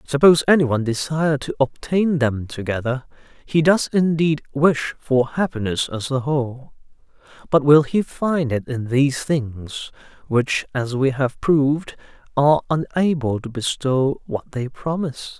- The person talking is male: Yes, male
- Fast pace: No, average, 140 wpm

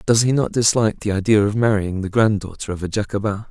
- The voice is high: No, low, 105 Hz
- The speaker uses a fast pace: Yes, fast, 220 wpm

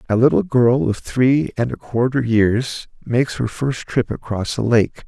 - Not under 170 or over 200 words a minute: Yes, average, 190 wpm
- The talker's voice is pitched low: Yes, low, 120 Hz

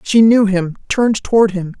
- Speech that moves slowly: No, average, 200 wpm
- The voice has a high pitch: Yes, high, 205 Hz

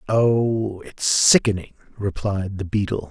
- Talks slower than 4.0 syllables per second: Yes, 3.8 syllables/s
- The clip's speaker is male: Yes, male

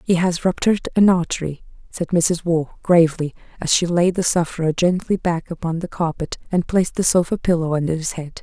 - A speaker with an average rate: Yes, average, 190 wpm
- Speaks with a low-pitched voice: No, medium, 170 Hz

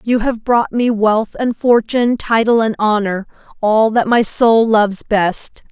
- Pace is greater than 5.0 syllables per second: No, 4.1 syllables/s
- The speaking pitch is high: Yes, high, 220 Hz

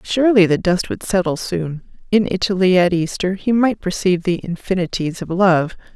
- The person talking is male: No, female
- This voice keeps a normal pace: Yes, average, 170 wpm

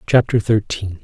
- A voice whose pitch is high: No, low, 105 Hz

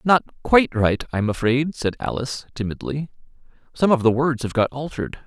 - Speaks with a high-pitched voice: No, low, 135 Hz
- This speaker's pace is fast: No, average, 170 wpm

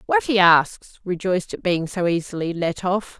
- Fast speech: No, average, 190 wpm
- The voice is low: No, medium, 185 Hz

